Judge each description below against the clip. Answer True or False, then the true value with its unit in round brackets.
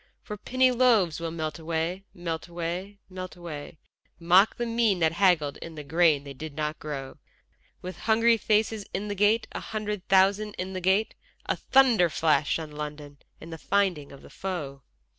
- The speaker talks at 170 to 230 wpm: True (180 wpm)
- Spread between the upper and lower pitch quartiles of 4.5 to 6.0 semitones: True (4.8 semitones)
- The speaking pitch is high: False (175 Hz)